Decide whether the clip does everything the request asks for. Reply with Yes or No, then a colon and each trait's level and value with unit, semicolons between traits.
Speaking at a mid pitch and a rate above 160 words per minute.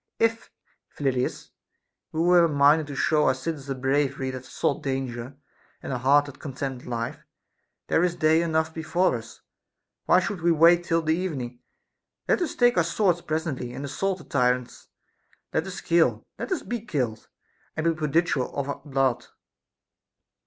Yes: medium, 150 Hz; average, 170 wpm